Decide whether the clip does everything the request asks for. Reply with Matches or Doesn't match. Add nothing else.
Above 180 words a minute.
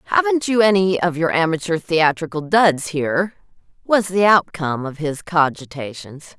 Doesn't match